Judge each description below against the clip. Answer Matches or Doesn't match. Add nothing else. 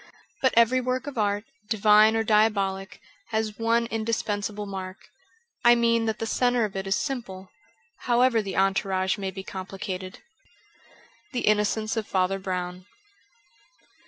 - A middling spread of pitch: Matches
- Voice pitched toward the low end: Doesn't match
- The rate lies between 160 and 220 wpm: Doesn't match